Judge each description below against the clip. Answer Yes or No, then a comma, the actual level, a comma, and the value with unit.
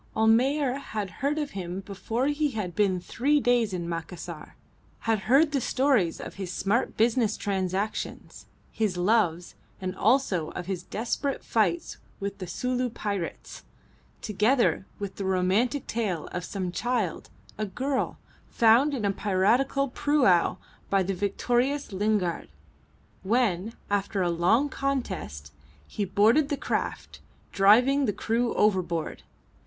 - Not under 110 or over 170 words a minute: Yes, slow, 135 wpm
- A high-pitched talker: Yes, high, 210 Hz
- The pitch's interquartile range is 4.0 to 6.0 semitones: Yes, average, 5.1 semitones